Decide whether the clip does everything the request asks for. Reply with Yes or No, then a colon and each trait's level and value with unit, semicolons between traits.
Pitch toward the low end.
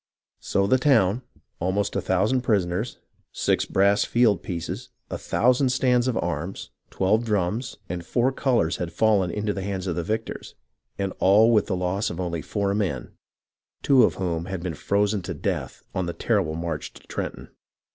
Yes: low, 100 Hz